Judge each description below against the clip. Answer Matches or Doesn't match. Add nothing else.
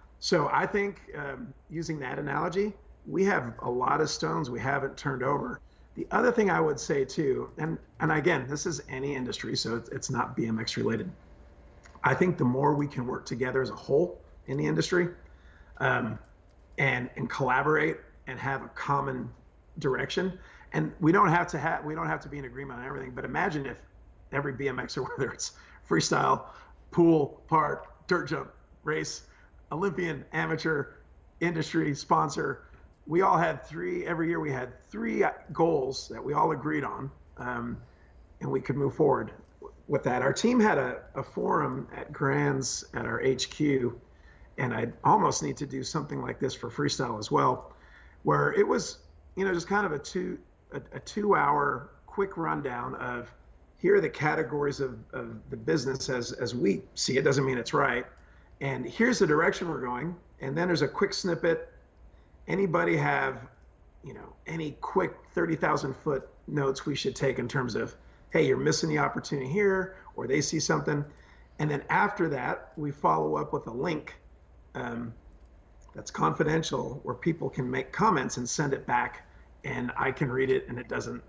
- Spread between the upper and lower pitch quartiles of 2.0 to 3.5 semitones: Doesn't match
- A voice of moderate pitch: Matches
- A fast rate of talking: Doesn't match